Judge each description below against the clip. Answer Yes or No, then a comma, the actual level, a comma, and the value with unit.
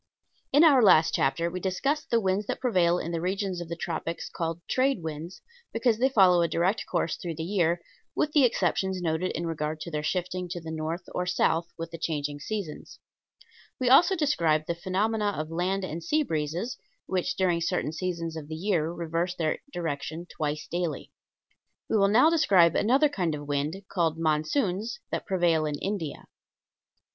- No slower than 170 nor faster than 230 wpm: Yes, average, 180 wpm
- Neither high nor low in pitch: Yes, medium, 175 Hz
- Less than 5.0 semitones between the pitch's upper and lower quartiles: Yes, average, 3.7 semitones